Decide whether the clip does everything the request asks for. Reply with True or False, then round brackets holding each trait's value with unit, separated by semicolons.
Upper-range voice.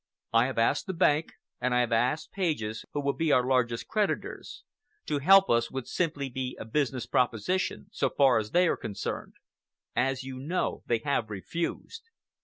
False (130 Hz)